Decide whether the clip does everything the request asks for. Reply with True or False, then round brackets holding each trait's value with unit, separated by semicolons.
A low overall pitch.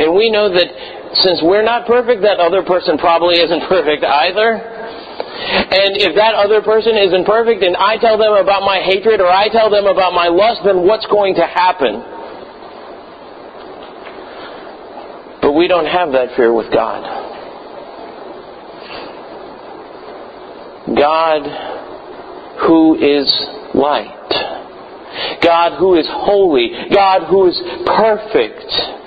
False (195 Hz)